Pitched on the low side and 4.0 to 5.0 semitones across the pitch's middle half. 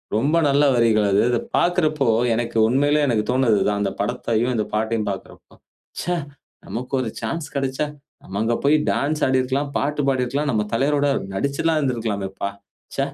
Yes: low, 130 Hz; average, 4.4 semitones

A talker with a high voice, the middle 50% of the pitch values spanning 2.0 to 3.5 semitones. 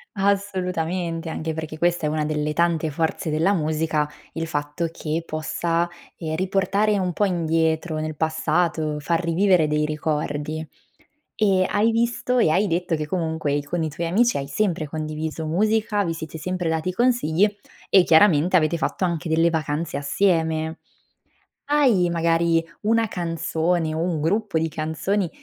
No: medium, 165 Hz; average, 2.8 semitones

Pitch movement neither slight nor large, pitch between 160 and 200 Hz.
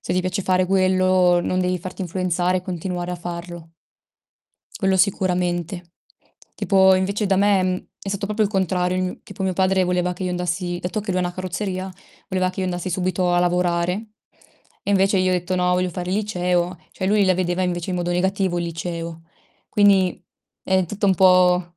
No: narrow, 1.2 semitones; medium, 185 Hz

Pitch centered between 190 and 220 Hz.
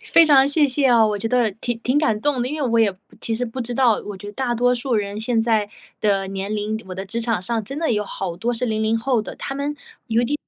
No: high, 230 Hz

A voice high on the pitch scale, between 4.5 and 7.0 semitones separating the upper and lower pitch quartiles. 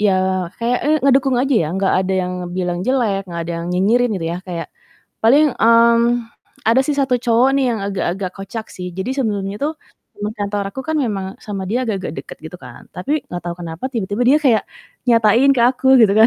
Yes: high, 220 Hz; average, 4.8 semitones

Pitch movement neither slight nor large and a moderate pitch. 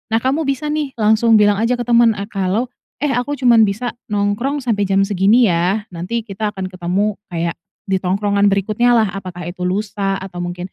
No: average, 3.7 semitones; high, 205 Hz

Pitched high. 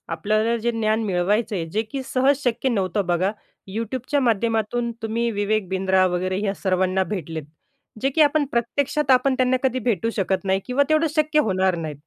Yes: high, 220 Hz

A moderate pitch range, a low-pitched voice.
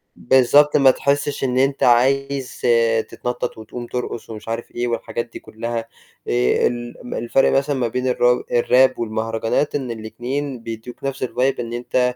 No: narrow, 2.3 semitones; low, 125 Hz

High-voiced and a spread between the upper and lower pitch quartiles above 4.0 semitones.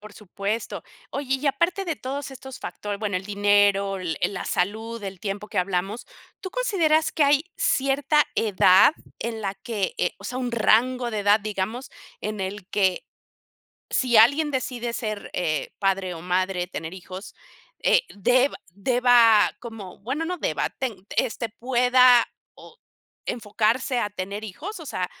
Yes: high, 220 Hz; average, 4.6 semitones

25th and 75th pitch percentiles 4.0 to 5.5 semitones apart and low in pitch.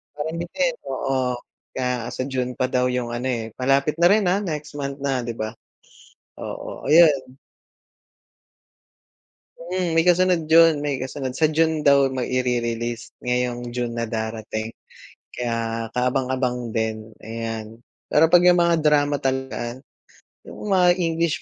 Yes: average, 4.9 semitones; low, 130 Hz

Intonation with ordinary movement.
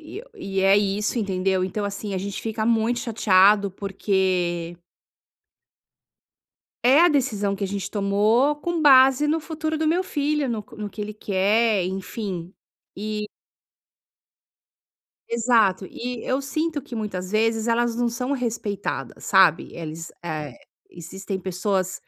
Yes: average, 4.3 semitones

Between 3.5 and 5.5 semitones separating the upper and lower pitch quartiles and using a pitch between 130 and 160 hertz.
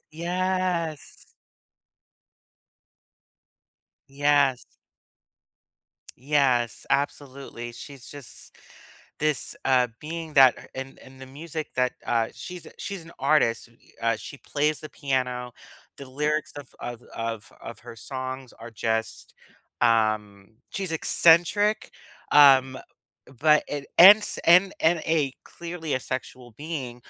Yes: average, 4.3 semitones; medium, 140 Hz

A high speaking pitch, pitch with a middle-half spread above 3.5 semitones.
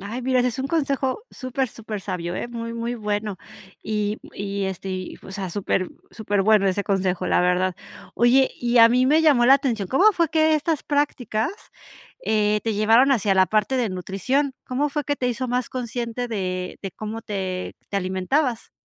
Yes: high, 225 Hz; average, 4.7 semitones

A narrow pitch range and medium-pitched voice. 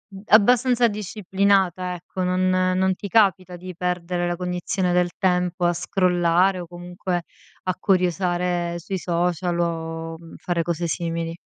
Yes: narrow, 1.4 semitones; medium, 180 Hz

